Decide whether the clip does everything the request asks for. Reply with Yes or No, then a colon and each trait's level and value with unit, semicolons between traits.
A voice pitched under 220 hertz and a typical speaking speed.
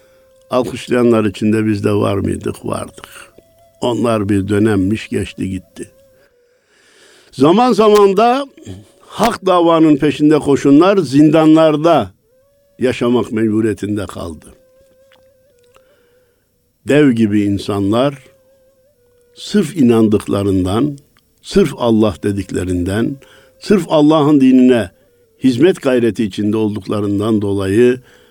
No: low, 135 Hz; slow, 85 wpm